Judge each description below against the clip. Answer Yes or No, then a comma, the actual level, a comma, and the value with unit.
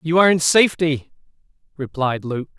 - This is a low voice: No, medium, 155 Hz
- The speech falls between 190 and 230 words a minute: No, average, 140 wpm